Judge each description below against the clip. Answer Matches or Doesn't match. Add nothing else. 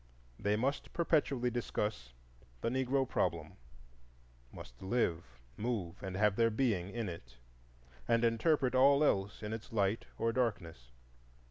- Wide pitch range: Matches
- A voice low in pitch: Matches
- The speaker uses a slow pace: Matches